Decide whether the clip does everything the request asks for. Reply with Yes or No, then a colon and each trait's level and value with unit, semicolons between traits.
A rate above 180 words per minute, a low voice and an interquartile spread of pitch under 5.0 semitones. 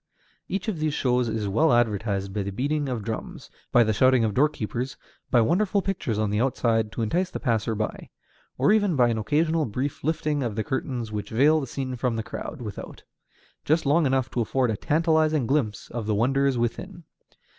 No: average, 200 wpm; low, 125 Hz; wide, 5.4 semitones